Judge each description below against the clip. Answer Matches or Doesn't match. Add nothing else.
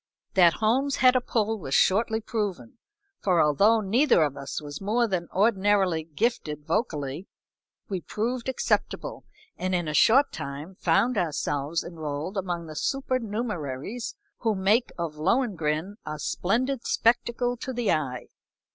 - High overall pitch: Matches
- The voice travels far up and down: Matches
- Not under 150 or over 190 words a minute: Doesn't match